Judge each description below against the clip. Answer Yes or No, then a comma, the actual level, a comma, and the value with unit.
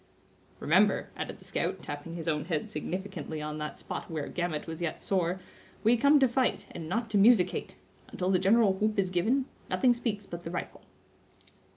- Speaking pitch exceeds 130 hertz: Yes, medium, 185 Hz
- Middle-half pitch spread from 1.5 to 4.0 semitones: No, average, 5.2 semitones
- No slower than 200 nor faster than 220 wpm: No, average, 185 wpm